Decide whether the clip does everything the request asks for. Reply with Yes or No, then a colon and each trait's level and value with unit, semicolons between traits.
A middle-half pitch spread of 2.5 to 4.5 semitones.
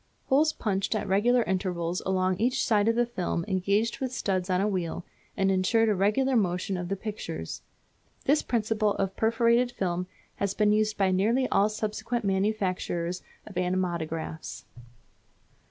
Yes: average, 3.4 semitones